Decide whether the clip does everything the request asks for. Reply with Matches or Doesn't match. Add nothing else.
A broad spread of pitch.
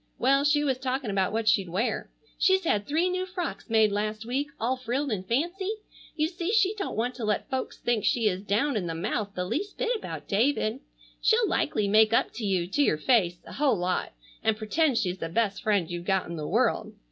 Matches